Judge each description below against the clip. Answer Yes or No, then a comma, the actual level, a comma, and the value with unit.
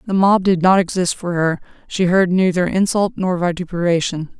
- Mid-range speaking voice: Yes, medium, 180 Hz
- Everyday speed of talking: Yes, average, 175 wpm